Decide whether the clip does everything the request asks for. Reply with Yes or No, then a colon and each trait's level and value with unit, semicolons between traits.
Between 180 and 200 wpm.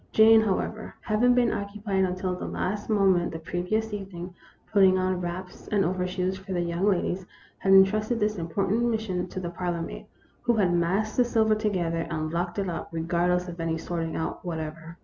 Yes: average, 190 wpm